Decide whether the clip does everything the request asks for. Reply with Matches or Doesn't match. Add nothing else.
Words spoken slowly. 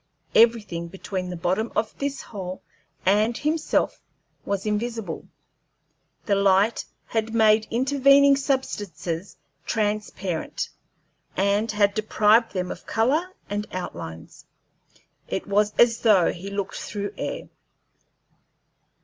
Matches